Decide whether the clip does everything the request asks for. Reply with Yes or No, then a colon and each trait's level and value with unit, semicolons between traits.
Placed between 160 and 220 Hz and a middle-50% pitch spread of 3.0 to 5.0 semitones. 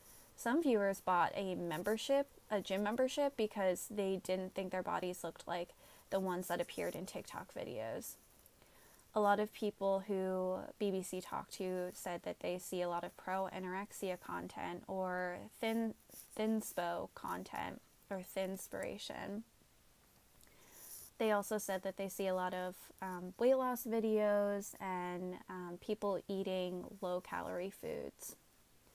No: high, 190 Hz; narrow, 2.4 semitones